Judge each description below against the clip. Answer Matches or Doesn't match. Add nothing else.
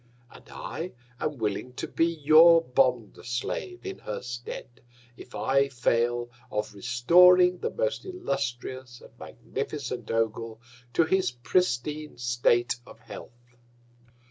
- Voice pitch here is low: Matches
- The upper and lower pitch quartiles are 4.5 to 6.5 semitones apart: Matches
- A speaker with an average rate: Doesn't match